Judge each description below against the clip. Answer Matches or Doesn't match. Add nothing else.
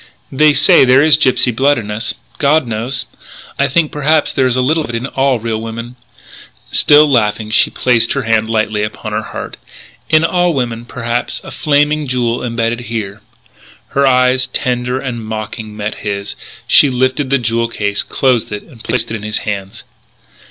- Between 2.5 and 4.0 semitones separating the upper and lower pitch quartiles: Matches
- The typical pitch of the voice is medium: Doesn't match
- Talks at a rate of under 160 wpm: Doesn't match